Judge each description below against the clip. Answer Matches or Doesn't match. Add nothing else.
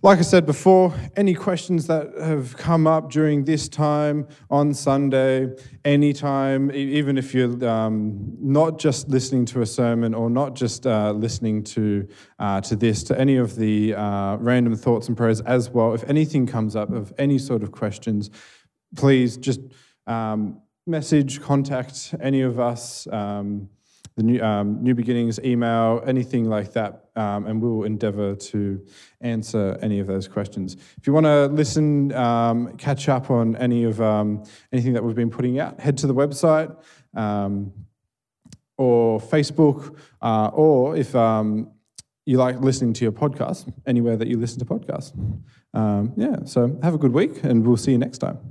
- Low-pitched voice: Matches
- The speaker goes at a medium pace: Matches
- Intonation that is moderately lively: Matches